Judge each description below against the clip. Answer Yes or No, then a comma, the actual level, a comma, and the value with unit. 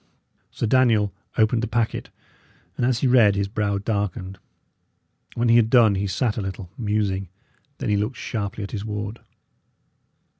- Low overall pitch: Yes, low, 105 Hz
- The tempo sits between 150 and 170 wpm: Yes, average, 160 wpm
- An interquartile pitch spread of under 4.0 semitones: Yes, narrow, 2.6 semitones